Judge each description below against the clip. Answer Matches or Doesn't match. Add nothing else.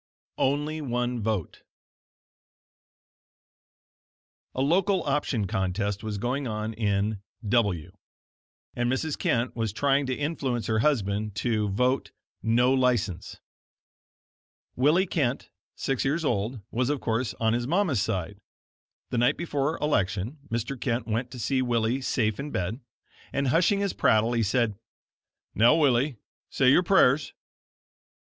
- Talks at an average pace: Doesn't match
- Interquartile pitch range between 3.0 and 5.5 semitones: Matches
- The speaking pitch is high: Doesn't match